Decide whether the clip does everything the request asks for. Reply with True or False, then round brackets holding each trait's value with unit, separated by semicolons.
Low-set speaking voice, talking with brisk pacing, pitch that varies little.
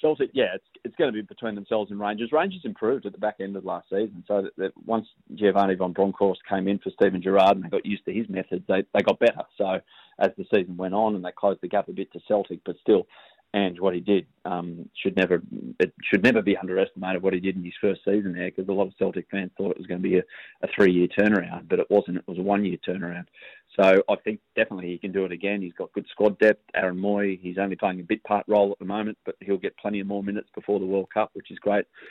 True (100 Hz; 275 wpm; 1.7 semitones)